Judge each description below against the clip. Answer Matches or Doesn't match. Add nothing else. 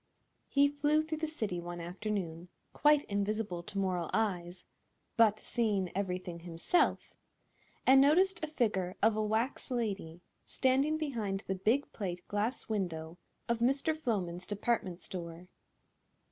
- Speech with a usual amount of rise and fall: Doesn't match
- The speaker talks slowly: Matches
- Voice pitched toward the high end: Matches